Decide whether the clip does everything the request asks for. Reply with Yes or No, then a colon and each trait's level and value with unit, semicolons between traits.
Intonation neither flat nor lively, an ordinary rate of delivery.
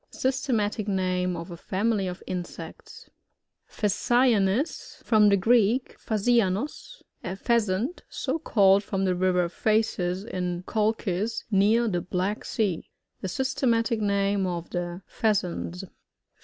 No: average, 3.7 semitones; slow, 125 wpm